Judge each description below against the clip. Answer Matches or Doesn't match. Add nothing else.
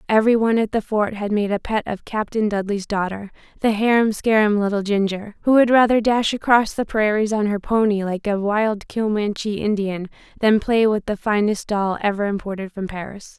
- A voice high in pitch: Matches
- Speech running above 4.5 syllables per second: Matches